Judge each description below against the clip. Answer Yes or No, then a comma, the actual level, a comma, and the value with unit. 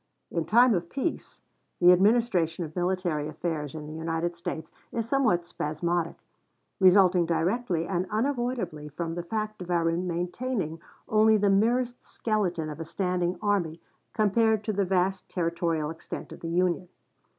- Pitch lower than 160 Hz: No, medium, 180 Hz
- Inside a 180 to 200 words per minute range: No, average, 150 wpm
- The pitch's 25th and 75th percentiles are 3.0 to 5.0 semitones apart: Yes, average, 4.3 semitones